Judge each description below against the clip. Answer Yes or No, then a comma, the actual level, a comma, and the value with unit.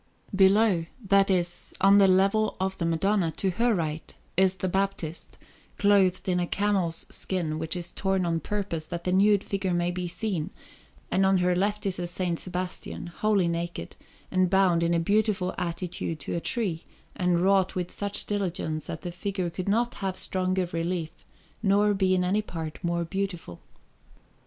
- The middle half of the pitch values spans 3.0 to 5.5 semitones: No, narrow, 2.4 semitones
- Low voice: No, medium, 185 Hz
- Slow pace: No, average, 175 wpm